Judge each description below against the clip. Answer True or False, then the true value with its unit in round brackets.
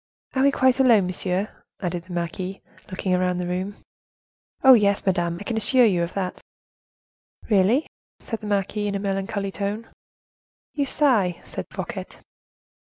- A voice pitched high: True (200 Hz)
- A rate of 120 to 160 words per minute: True (155 wpm)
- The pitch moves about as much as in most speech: True (3.4 semitones)